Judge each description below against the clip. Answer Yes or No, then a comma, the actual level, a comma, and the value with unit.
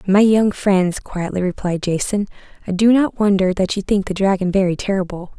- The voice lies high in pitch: Yes, high, 195 Hz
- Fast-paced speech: No, average, 190 wpm